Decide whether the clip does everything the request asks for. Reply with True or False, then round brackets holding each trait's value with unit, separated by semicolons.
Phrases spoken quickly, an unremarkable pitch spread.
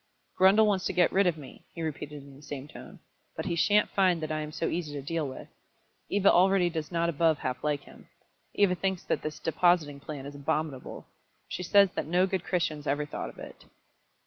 True (215 wpm; 3.7 semitones)